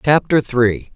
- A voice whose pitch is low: Yes, low, 125 Hz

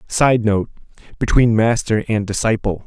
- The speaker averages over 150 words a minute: No, slow, 105 wpm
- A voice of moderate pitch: No, low, 110 Hz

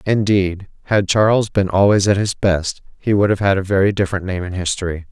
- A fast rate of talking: Yes, fast, 210 wpm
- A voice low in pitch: Yes, very low, 95 Hz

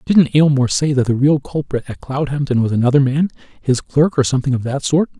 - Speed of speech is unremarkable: No, fast, 210 wpm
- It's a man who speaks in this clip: Yes, male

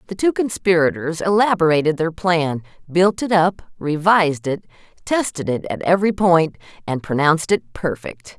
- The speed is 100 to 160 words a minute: Yes, average, 145 wpm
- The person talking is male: No, female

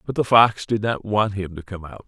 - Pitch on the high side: No, low, 100 Hz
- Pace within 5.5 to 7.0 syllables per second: No, 5.2 syllables/s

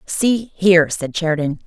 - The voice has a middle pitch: Yes, medium, 175 Hz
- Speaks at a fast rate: No, average, 145 wpm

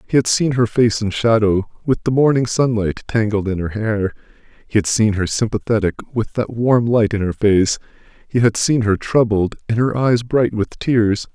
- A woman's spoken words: No, male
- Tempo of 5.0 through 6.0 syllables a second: No, 4.8 syllables/s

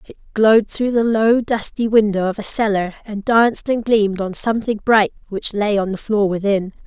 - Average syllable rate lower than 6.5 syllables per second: Yes, 5.2 syllables/s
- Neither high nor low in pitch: No, high, 210 Hz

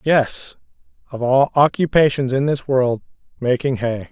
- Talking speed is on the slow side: Yes, slow, 130 wpm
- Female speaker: No, male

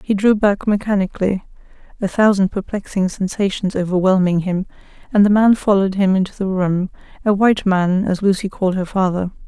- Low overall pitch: No, high, 195 Hz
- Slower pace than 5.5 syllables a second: No, 5.7 syllables/s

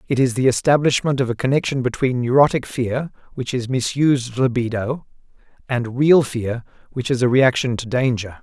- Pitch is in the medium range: No, low, 125 Hz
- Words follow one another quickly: No, average, 165 wpm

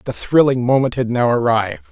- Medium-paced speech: Yes, average, 190 wpm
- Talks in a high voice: No, low, 125 Hz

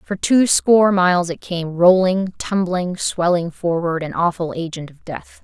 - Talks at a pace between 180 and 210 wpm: No, average, 165 wpm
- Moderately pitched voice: Yes, medium, 175 Hz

